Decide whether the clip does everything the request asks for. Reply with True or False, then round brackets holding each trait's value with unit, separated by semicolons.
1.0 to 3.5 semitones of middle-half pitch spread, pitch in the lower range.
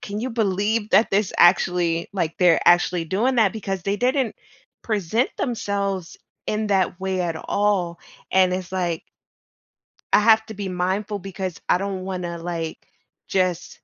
False (2.7 semitones; 190 Hz)